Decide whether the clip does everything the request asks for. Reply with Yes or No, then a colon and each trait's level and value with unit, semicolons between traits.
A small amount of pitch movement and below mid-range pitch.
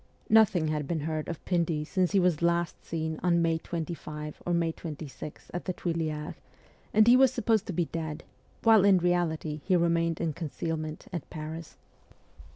No: narrow, 2.2 semitones; medium, 170 Hz